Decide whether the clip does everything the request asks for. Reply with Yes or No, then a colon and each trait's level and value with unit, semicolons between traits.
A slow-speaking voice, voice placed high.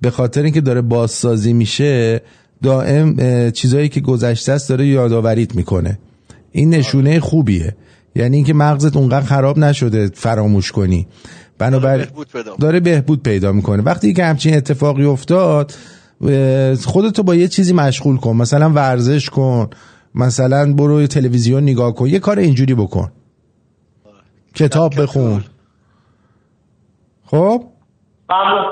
No: slow, 115 wpm; low, 130 Hz